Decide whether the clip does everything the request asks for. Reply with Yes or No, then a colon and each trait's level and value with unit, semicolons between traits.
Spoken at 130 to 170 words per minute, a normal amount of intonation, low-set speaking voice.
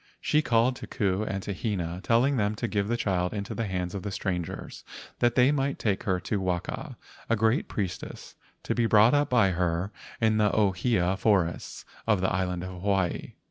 No: average, 195 wpm; average, 3.8 semitones; low, 100 Hz